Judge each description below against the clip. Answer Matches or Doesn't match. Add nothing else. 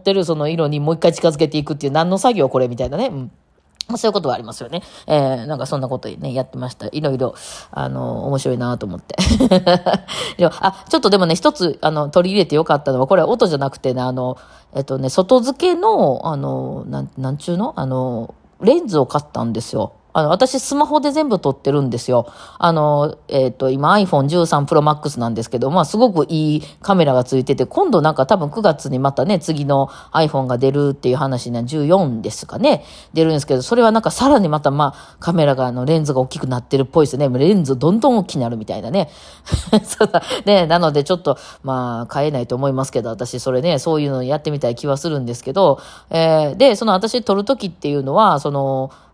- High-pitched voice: Doesn't match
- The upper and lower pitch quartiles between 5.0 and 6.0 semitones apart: Matches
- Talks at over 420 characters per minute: Matches